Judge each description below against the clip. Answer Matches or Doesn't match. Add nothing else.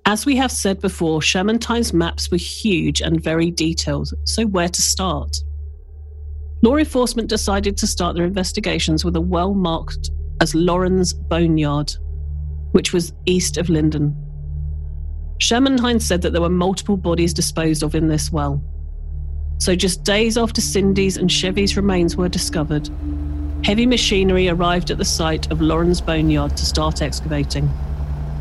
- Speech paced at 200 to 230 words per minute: Doesn't match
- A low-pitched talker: Doesn't match